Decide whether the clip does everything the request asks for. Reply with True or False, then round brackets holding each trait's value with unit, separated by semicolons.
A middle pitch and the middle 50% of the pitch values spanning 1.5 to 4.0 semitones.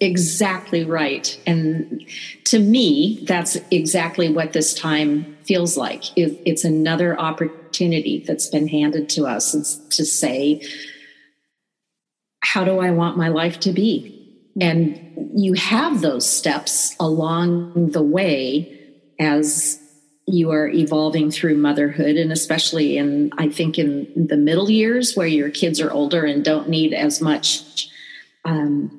True (160 Hz; 2.4 semitones)